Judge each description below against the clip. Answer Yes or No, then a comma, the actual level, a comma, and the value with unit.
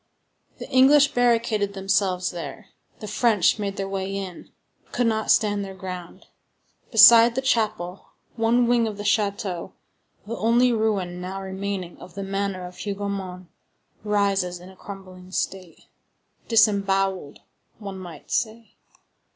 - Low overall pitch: No, high, 200 Hz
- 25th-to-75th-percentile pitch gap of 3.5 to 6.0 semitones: No, average, 2.9 semitones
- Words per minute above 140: No, slow, 135 wpm